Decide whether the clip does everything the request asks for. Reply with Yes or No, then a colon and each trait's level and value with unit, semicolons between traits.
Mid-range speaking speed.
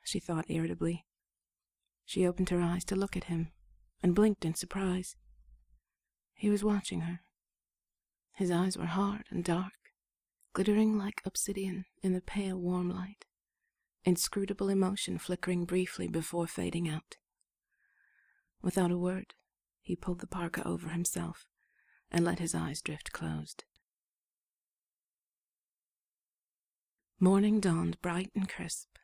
No: slow, 125 wpm